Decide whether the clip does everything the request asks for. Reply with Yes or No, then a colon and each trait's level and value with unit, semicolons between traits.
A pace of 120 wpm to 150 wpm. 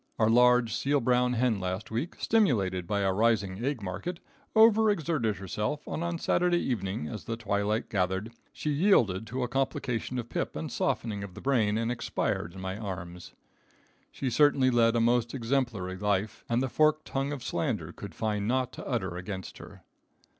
No: average, 180 wpm